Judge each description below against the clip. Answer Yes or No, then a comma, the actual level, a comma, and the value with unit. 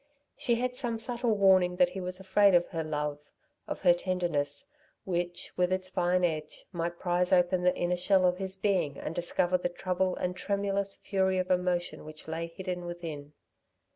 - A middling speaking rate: Yes, average, 180 wpm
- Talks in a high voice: No, medium, 180 Hz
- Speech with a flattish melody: Yes, narrow, 1.5 semitones